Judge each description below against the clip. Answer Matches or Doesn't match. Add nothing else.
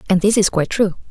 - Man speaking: Doesn't match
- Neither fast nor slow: Doesn't match